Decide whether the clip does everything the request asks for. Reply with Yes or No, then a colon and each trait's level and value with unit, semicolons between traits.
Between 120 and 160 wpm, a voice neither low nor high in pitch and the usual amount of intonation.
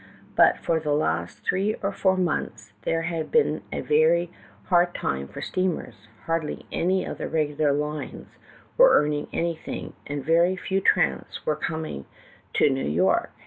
Yes: average, 155 wpm; medium, 165 Hz; average, 3.9 semitones